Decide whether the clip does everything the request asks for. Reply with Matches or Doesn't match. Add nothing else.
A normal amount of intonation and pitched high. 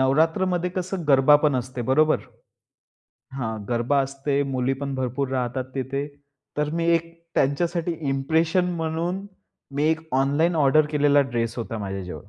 Doesn't match